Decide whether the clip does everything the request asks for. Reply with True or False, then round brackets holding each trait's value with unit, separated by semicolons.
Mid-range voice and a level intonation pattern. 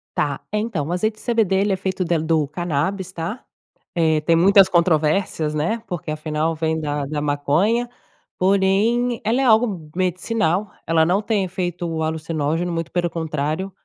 False (175 Hz; 3.9 semitones)